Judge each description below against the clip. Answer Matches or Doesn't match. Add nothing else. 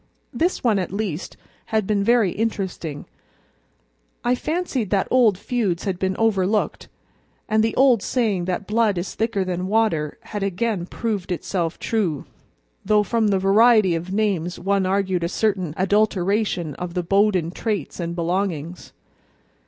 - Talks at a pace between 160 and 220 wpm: Doesn't match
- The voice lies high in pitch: Matches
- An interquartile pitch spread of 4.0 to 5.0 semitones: Doesn't match